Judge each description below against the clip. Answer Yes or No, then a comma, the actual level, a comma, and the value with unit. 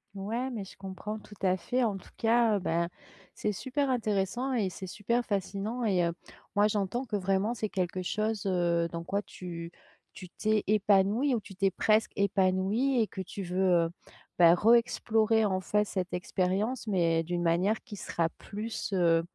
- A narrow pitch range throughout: No, average, 3.2 semitones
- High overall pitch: Yes, high, 200 Hz